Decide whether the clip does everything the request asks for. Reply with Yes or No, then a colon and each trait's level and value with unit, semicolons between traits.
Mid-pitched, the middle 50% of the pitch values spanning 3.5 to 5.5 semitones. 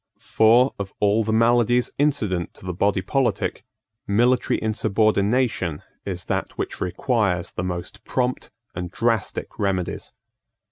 No: low, 105 Hz; average, 4.4 semitones